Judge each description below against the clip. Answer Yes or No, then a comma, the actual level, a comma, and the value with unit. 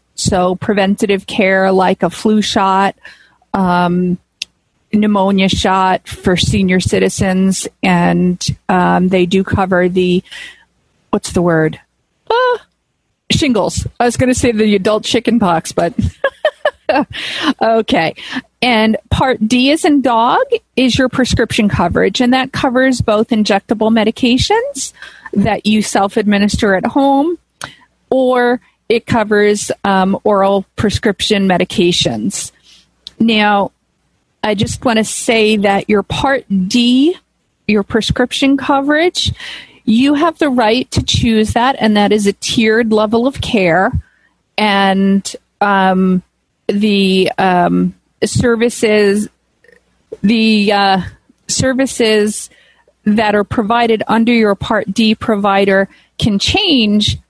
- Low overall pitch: No, high, 215 Hz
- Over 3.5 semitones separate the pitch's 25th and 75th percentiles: Yes, average, 4.1 semitones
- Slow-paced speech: Yes, slow, 115 wpm